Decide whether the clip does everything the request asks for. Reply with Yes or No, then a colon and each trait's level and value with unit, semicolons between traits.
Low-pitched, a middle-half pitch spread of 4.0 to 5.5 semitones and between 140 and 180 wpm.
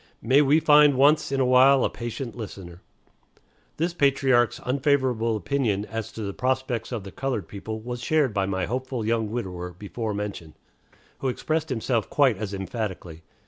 Yes: low, 120 Hz; average, 4.6 semitones; average, 165 wpm